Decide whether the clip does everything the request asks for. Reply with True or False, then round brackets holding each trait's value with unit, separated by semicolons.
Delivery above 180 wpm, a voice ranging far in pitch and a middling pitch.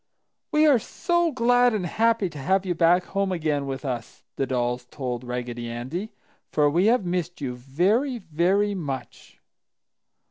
False (155 wpm; 7.9 semitones; 175 Hz)